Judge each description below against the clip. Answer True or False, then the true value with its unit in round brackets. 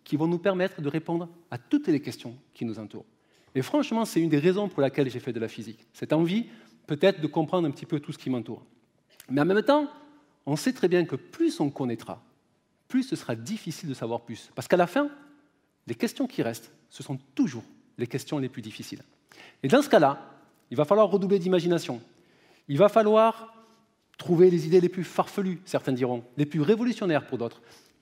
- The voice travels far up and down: True (7.8 semitones)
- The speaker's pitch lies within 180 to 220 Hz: False (155 Hz)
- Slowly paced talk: False (210 wpm)